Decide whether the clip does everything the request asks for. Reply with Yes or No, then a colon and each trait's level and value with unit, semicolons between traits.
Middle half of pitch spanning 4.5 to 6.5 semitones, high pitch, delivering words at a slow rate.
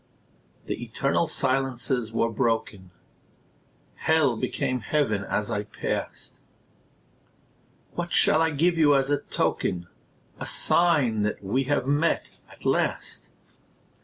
No: average, 5.0 semitones; low, 130 Hz; slow, 115 wpm